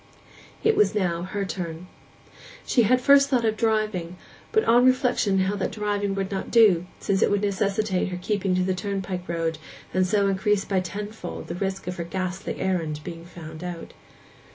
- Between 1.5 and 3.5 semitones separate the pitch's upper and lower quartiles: Yes, average, 2.8 semitones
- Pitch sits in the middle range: No, high, 195 Hz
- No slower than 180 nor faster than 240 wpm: Yes, average, 185 wpm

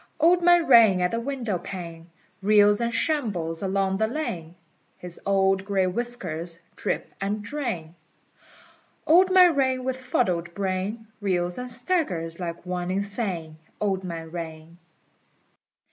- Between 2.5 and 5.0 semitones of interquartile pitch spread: No, wide, 5.6 semitones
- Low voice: No, high, 195 Hz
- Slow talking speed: Yes, slow, 130 wpm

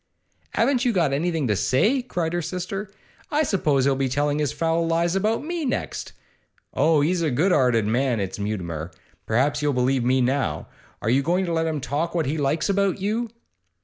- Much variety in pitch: Yes, wide, 5.7 semitones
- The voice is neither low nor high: Yes, medium, 155 Hz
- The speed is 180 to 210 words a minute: Yes, average, 195 wpm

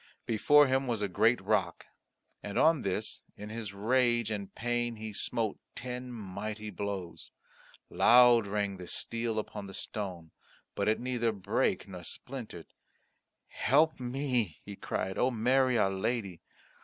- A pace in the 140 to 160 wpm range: Yes, average, 145 wpm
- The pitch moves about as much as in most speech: Yes, average, 3.6 semitones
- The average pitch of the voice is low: Yes, low, 110 Hz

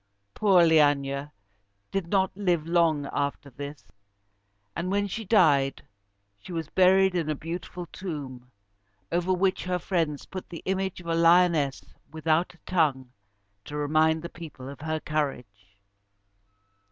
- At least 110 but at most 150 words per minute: Yes, average, 140 wpm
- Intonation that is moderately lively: Yes, average, 3.9 semitones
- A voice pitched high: No, medium, 165 Hz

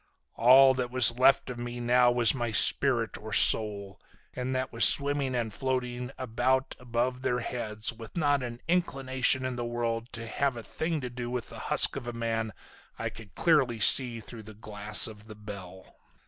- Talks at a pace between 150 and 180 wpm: No, average, 190 wpm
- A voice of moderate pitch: No, low, 120 Hz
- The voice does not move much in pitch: Yes, narrow, 2.3 semitones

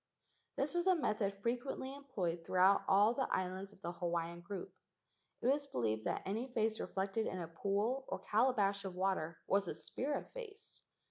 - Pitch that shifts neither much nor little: No, wide, 6.2 semitones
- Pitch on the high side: Yes, high, 200 Hz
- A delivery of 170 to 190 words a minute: Yes, average, 175 wpm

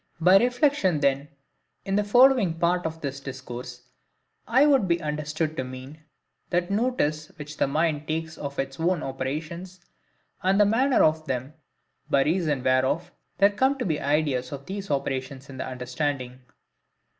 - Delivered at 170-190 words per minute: No, average, 155 wpm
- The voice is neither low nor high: Yes, medium, 155 Hz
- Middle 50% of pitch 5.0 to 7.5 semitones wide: Yes, wide, 5.5 semitones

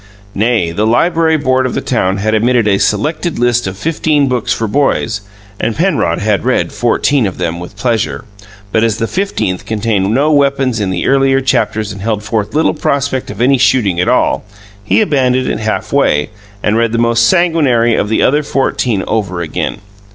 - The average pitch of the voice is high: No, low, 115 Hz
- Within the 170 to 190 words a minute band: Yes, average, 185 wpm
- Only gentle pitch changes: No, average, 4.5 semitones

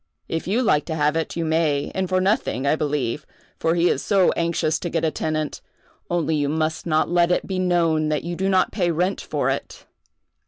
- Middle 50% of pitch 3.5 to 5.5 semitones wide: No, narrow, 2.4 semitones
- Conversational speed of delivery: No, fast, 220 wpm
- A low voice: No, medium, 165 Hz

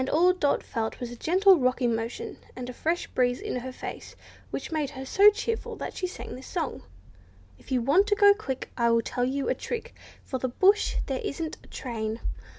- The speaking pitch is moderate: No, very high, 265 Hz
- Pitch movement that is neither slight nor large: No, wide, 6.7 semitones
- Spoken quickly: Yes, fast, 215 wpm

